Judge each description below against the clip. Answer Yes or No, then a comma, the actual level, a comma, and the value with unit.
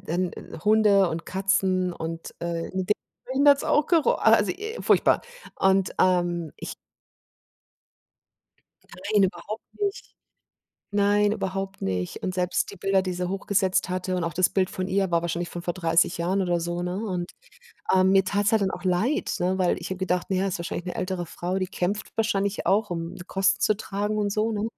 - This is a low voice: No, high, 190 Hz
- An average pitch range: No, narrow, 2.3 semitones